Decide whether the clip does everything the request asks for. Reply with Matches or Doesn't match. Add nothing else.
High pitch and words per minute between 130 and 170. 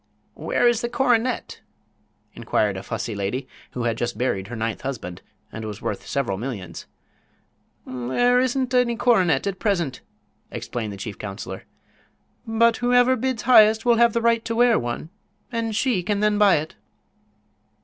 Matches